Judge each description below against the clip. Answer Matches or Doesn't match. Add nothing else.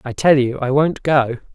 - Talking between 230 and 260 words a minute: Matches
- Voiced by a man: Matches